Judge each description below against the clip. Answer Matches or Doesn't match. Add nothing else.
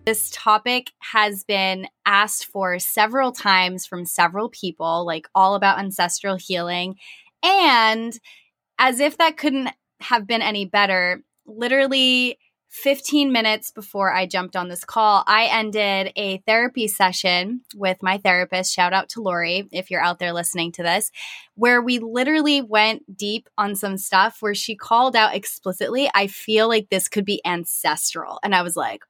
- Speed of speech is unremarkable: Matches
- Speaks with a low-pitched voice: Doesn't match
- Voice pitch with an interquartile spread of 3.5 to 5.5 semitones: Matches